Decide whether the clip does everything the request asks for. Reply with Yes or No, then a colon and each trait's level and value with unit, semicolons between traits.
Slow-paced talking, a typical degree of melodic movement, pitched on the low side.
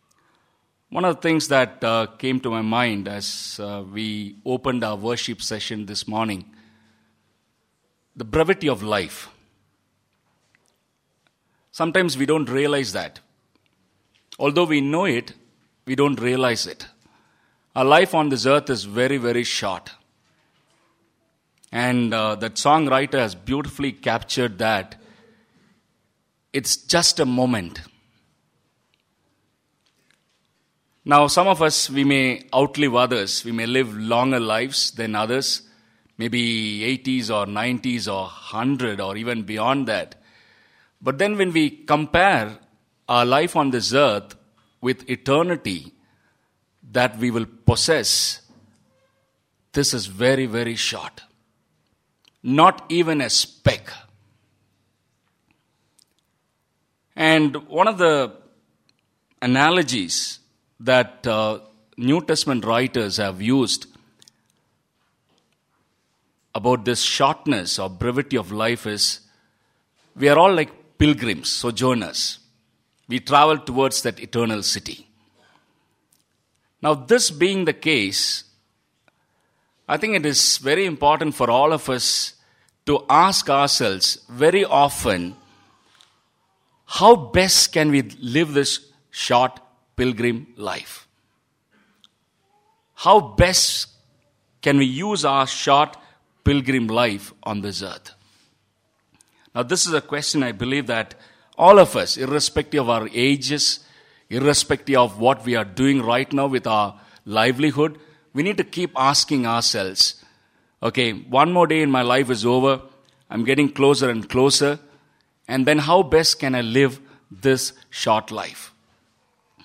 Yes: slow, 120 wpm; average, 4.2 semitones; low, 130 Hz